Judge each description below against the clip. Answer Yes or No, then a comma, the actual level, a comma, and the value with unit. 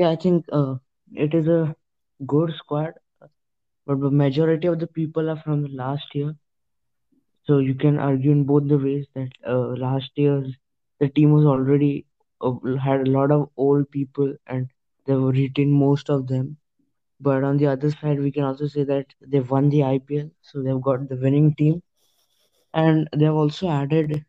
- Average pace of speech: Yes, average, 180 wpm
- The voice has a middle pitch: Yes, medium, 145 Hz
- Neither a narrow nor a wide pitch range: No, narrow, 1.8 semitones